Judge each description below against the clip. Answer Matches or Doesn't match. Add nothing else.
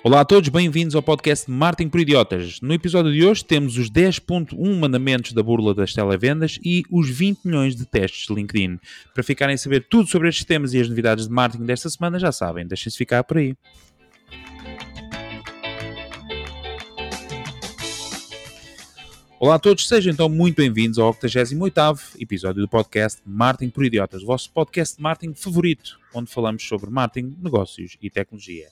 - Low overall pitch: Matches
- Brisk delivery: Doesn't match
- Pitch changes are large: Matches